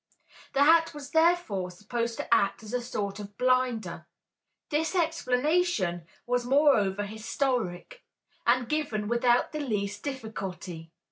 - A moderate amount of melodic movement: No, wide, 5.9 semitones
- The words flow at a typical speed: No, slow, 125 wpm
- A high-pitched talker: Yes, high, 240 Hz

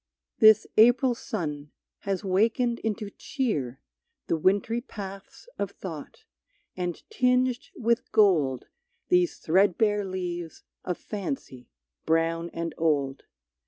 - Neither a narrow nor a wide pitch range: No, wide, 5.8 semitones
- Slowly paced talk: Yes, slow, 105 wpm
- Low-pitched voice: No, high, 195 Hz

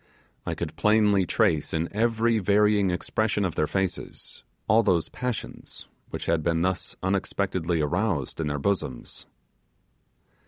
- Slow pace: Yes, slow, 130 wpm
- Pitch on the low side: Yes, very low, 95 Hz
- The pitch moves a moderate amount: Yes, average, 4.3 semitones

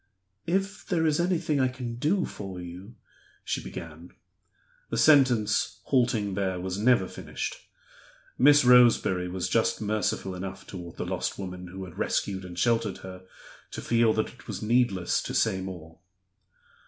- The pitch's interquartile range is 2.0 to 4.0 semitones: No, wide, 5.4 semitones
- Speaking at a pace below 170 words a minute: Yes, average, 155 wpm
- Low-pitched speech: Yes, low, 105 Hz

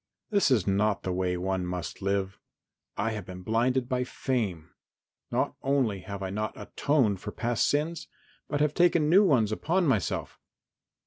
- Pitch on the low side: Yes, low, 110 Hz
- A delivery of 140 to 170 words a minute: Yes, average, 165 wpm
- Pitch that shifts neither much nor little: No, wide, 6.5 semitones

